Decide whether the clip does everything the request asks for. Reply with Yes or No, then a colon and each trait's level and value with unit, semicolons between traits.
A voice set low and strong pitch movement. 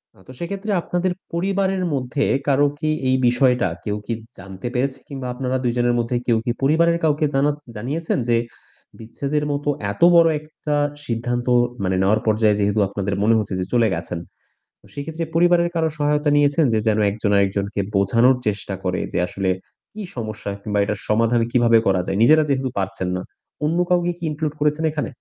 Yes: low, 125 Hz; wide, 6.3 semitones